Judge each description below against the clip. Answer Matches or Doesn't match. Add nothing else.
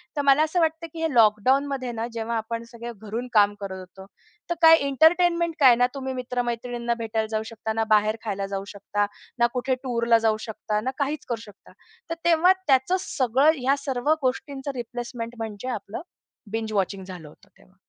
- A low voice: Doesn't match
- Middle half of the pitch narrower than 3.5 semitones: Doesn't match